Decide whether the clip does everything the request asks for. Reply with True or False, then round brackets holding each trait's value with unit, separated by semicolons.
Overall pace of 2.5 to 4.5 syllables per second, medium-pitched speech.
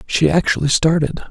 False (5.0 syllables/s; 155 Hz)